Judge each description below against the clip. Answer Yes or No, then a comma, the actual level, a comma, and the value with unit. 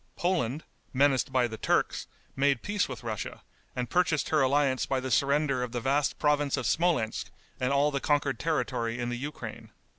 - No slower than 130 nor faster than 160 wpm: No, average, 180 wpm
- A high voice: No, low, 135 Hz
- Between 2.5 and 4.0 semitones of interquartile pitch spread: Yes, average, 2.9 semitones